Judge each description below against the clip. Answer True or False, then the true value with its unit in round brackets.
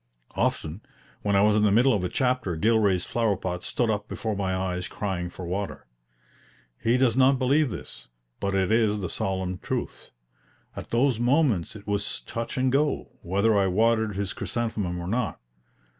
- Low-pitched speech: True (105 Hz)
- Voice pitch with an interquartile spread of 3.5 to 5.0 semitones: True (4.0 semitones)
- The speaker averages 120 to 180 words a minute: True (175 wpm)